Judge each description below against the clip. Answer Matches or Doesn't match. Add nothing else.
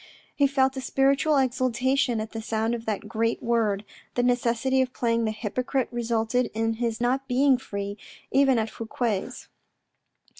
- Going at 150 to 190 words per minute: Matches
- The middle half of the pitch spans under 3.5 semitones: Matches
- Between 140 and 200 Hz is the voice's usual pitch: Doesn't match